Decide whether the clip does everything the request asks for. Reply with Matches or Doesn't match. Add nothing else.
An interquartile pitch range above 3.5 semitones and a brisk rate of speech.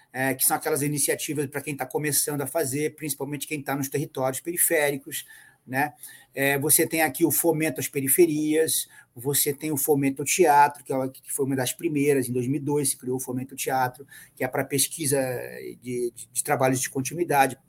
Doesn't match